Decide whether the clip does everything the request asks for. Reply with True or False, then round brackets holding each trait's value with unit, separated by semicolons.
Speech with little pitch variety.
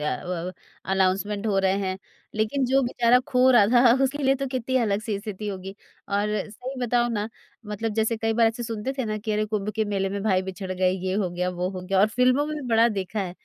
False (3.8 semitones)